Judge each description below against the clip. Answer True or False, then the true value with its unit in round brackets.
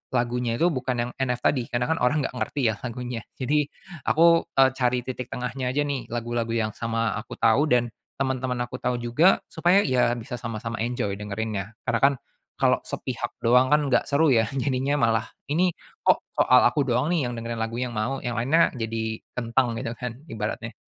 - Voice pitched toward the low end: True (125 Hz)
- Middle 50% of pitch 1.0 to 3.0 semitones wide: True (2.7 semitones)